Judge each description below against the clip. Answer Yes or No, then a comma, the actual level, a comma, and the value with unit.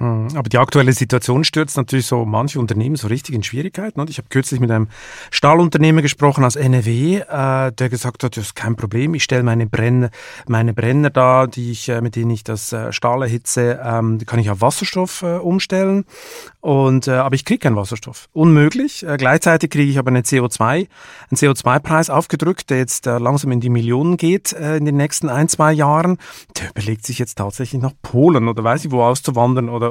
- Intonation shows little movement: No, average, 4.4 semitones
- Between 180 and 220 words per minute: Yes, average, 185 wpm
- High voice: No, low, 130 Hz